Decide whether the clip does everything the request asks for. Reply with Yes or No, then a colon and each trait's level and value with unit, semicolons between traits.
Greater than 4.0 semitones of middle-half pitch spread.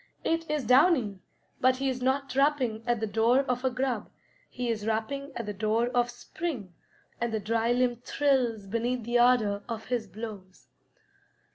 No: average, 2.9 semitones